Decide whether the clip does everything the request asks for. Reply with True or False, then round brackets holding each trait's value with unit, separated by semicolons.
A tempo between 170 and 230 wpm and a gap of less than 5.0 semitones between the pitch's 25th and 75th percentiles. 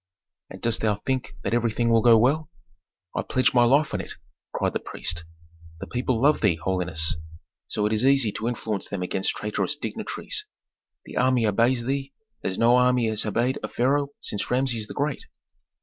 True (180 wpm; 3.5 semitones)